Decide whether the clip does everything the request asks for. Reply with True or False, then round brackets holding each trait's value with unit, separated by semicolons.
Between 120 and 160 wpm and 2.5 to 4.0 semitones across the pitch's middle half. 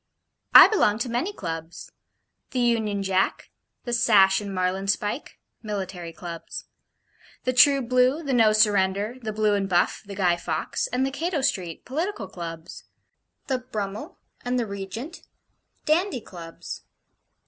False (140 wpm; 4.8 semitones)